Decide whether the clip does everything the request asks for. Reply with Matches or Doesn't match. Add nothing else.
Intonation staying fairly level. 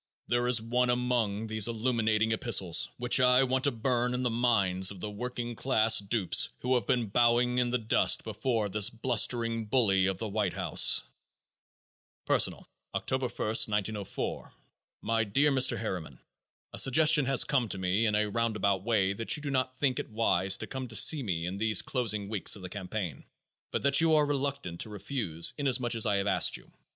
Doesn't match